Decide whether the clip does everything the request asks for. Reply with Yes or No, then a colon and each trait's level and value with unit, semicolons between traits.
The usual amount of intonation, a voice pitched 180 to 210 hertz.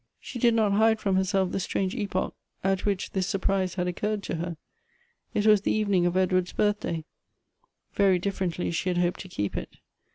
No: narrow, 2.3 semitones; high, 190 Hz